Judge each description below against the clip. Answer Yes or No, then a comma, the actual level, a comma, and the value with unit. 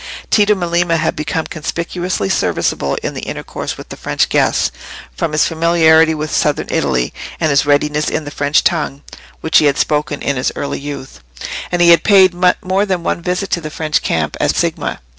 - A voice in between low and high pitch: Yes, medium, 160 Hz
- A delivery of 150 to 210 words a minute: Yes, average, 190 wpm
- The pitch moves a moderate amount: Yes, average, 3.0 semitones